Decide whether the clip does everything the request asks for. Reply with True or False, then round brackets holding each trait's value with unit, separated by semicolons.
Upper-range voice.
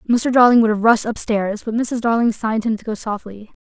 True (225 Hz)